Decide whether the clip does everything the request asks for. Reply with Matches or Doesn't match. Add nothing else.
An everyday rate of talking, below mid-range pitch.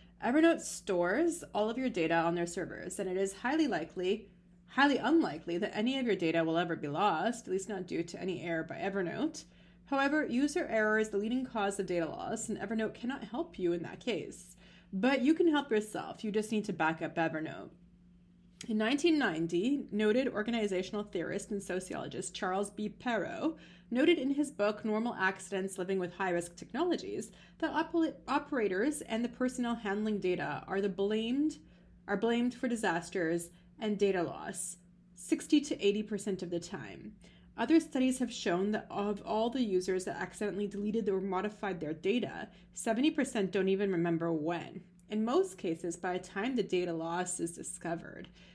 Doesn't match